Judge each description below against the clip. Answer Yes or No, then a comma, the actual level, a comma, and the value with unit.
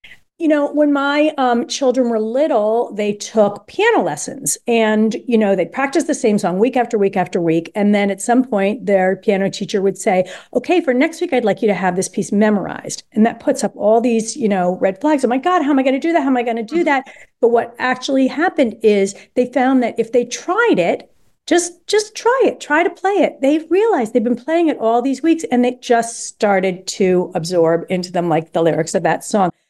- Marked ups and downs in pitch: Yes, wide, 6.0 semitones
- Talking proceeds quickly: Yes, fast, 235 wpm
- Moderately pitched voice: No, high, 235 Hz